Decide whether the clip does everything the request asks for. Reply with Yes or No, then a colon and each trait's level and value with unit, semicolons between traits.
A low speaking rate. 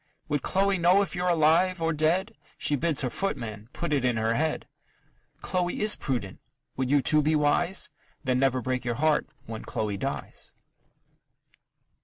No: average, 165 wpm